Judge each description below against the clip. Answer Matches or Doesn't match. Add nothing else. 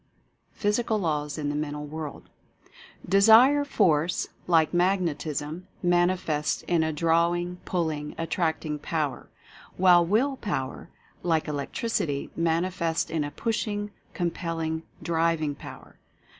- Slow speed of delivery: Matches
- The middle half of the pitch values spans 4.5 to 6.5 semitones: Doesn't match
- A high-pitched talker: Doesn't match